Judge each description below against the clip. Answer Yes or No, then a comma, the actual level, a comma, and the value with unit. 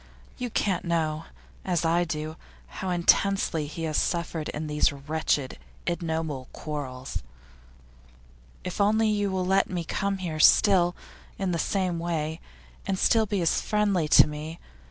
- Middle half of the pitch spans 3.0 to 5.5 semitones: Yes, average, 3.6 semitones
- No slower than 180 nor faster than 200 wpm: No, average, 145 wpm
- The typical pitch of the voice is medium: Yes, medium, 170 Hz